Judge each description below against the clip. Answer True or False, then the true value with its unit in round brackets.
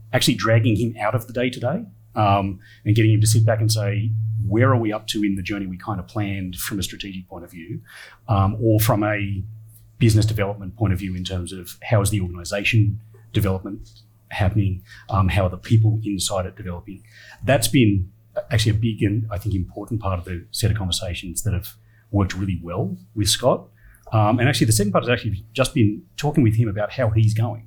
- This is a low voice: True (110 Hz)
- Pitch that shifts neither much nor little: False (2.3 semitones)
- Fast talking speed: True (215 wpm)